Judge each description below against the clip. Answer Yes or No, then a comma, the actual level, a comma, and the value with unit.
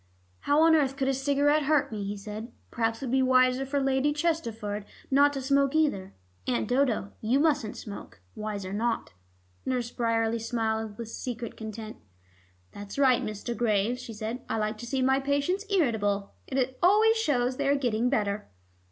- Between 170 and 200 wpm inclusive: Yes, average, 175 wpm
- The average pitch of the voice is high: Yes, very high, 250 Hz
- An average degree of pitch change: Yes, average, 4.3 semitones